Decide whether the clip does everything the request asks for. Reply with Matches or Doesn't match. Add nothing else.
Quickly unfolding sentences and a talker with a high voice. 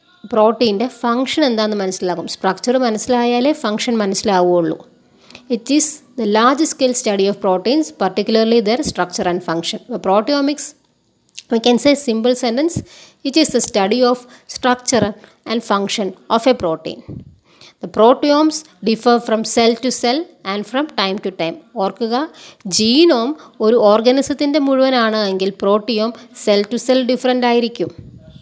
Matches